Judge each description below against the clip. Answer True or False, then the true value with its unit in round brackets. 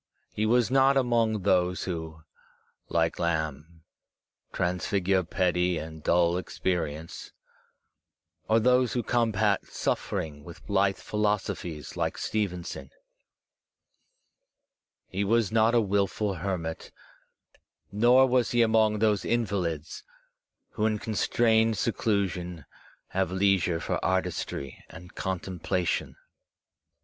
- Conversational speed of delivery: False (100 wpm)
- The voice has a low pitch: True (95 Hz)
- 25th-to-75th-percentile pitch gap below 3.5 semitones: False (4.2 semitones)